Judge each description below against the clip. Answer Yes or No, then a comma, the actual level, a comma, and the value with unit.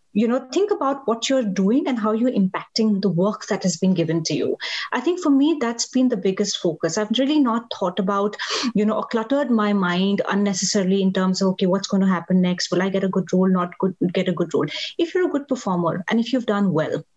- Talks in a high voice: Yes, high, 205 Hz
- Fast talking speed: Yes, fast, 250 wpm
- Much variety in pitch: No, average, 4.3 semitones